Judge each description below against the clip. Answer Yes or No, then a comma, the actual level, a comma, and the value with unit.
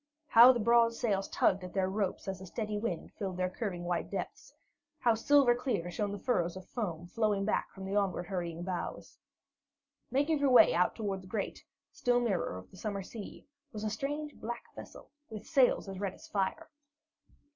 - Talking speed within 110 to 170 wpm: No, average, 190 wpm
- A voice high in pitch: Yes, high, 205 Hz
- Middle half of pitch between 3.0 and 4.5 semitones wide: Yes, average, 4.1 semitones